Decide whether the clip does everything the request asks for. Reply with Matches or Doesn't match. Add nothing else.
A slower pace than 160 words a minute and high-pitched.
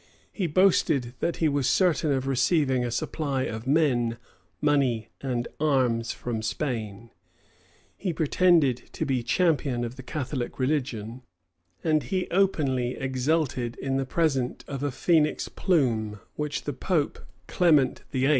Doesn't match